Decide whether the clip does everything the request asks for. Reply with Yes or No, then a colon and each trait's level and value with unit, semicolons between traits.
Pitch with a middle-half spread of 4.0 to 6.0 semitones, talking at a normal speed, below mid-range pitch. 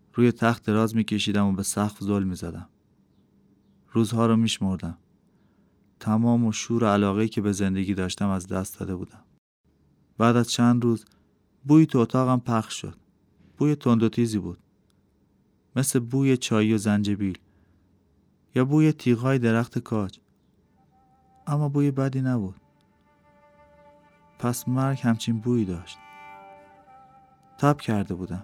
Yes: average, 4.5 semitones; average, 130 wpm; low, 115 Hz